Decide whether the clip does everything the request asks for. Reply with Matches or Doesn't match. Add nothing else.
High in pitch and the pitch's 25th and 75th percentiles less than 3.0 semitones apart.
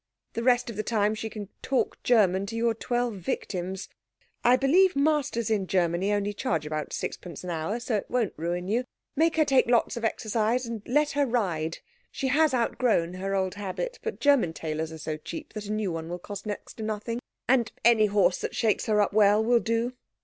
Doesn't match